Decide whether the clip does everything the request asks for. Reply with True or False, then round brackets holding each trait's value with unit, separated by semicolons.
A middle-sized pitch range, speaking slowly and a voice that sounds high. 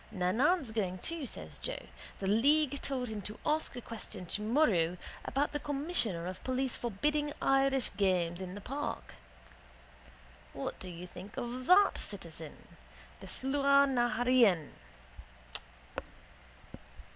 False (6.8 semitones; 130 wpm; 240 Hz)